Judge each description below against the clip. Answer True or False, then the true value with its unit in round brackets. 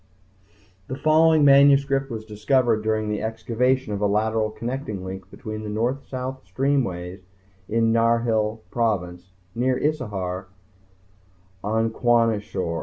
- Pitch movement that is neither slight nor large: True (3.7 semitones)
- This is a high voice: False (115 Hz)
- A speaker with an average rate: False (120 wpm)